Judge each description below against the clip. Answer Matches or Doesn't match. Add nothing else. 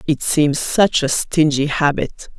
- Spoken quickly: Doesn't match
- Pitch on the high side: Doesn't match